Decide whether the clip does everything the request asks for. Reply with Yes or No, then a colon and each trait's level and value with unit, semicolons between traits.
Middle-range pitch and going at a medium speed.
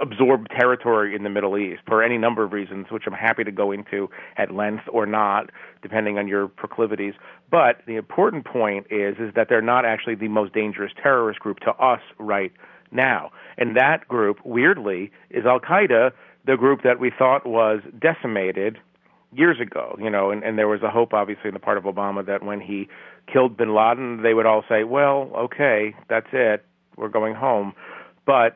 No: low, 110 Hz; average, 195 wpm